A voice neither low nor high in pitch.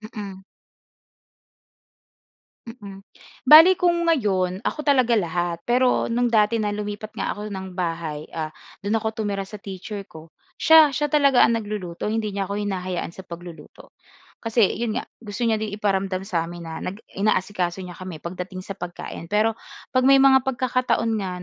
No: high, 205 Hz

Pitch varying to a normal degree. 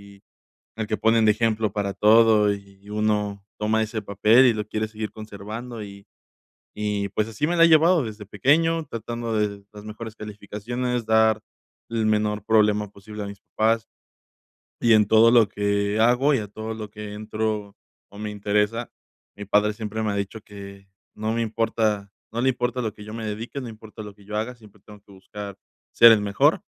No: narrow, 1.6 semitones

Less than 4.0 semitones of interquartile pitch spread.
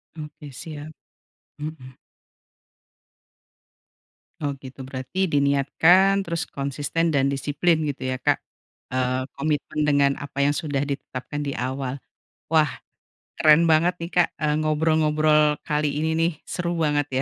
Yes: narrow, 2.4 semitones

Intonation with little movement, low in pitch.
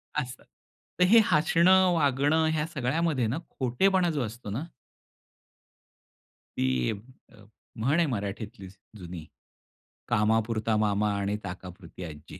No: wide, 7.3 semitones; low, 120 Hz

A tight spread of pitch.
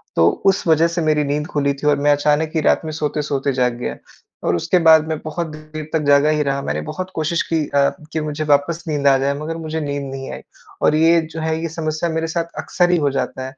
Yes: narrow, 2.2 semitones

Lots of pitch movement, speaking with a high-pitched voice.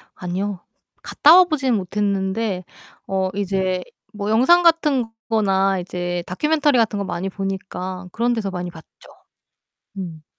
No: average, 3.8 semitones; high, 195 Hz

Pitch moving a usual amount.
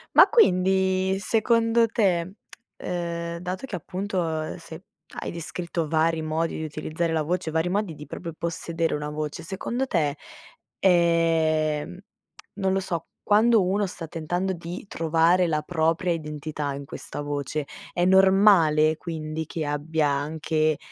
Yes: average, 3.0 semitones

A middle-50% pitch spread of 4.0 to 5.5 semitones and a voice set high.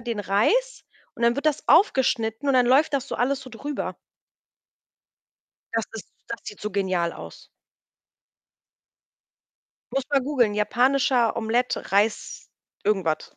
Yes: average, 4.4 semitones; high, 240 Hz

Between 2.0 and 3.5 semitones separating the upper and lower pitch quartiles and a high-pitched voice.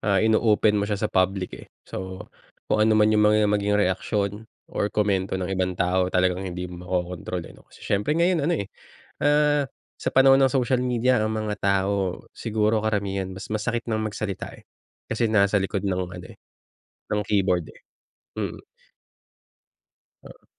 No: average, 2.7 semitones; low, 105 Hz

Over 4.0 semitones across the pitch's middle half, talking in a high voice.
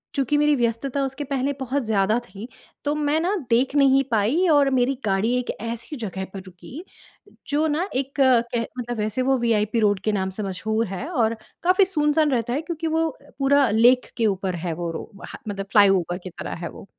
Yes: average, 5.3 semitones; high, 240 Hz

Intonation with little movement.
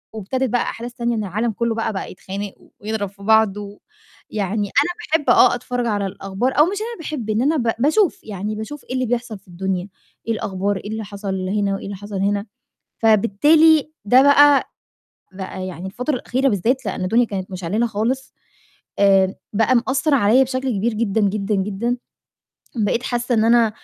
No: average, 3.9 semitones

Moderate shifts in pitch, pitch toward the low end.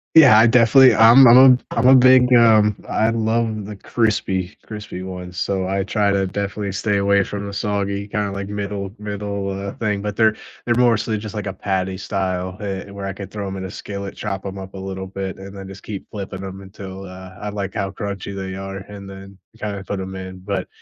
No: narrow, 1.6 semitones; low, 100 Hz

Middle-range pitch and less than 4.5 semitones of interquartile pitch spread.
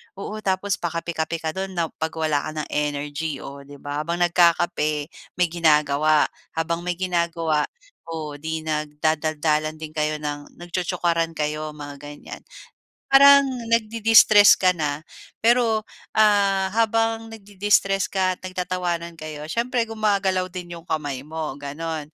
Yes: medium, 165 Hz; average, 4.0 semitones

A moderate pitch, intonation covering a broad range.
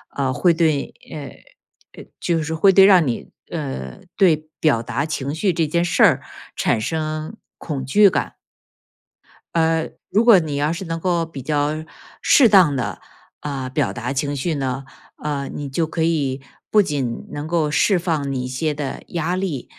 No: medium, 155 Hz; average, 3.5 semitones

